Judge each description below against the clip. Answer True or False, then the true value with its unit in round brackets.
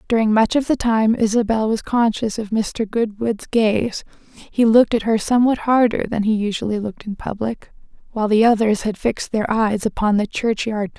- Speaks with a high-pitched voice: True (220 Hz)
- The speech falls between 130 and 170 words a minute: False (190 wpm)